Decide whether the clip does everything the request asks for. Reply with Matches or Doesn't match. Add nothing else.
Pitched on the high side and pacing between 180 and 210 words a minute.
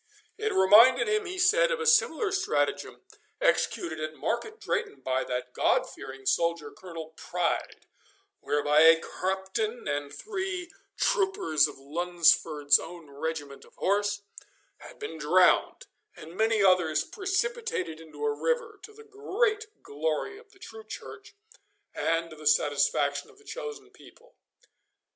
Doesn't match